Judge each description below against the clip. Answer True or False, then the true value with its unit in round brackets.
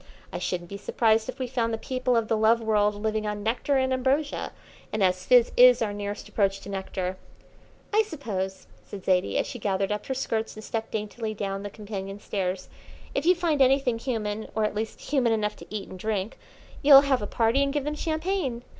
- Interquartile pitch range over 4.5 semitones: False (4.1 semitones)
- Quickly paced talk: True (215 wpm)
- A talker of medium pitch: False (220 Hz)